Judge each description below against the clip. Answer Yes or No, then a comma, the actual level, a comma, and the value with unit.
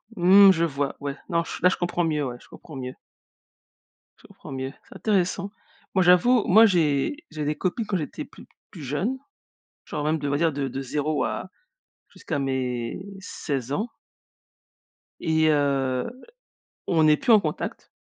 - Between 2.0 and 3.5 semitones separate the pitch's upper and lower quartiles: No, average, 4.8 semitones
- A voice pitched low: No, medium, 155 Hz